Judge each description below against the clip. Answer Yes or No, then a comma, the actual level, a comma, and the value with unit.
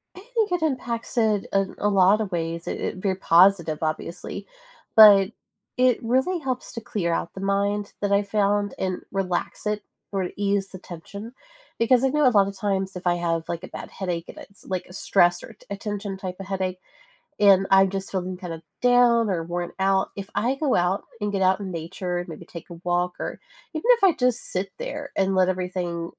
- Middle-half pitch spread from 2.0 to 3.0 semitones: Yes, average, 2.7 semitones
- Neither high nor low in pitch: No, high, 195 Hz